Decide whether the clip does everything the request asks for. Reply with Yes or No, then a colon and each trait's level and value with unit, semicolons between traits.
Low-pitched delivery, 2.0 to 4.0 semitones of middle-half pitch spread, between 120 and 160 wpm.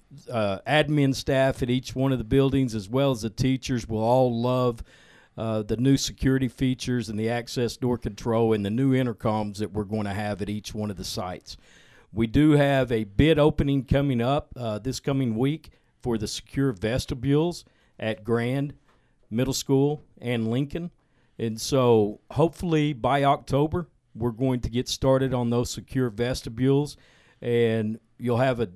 No: low, 125 Hz; average, 3.3 semitones; average, 170 wpm